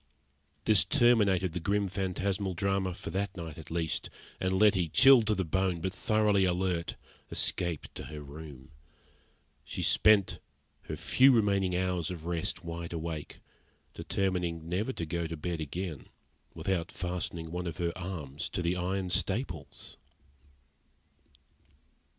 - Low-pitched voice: Yes, very low, 90 Hz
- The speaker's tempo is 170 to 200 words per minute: No, average, 140 wpm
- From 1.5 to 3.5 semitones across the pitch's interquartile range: Yes, narrow, 2.6 semitones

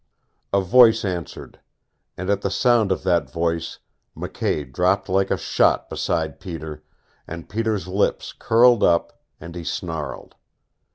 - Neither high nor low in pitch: No, very low, 90 Hz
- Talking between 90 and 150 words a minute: Yes, slow, 135 wpm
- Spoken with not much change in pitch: No, average, 3.4 semitones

